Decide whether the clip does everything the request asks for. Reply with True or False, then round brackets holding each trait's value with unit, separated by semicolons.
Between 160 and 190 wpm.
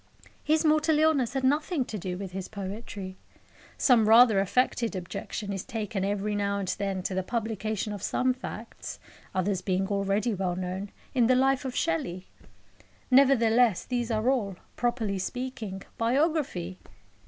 False (150 wpm)